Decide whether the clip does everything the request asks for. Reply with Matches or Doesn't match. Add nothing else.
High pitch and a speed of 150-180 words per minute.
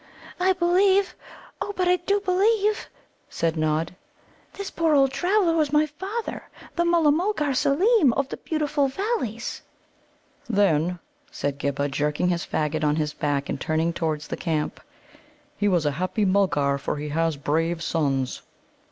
Matches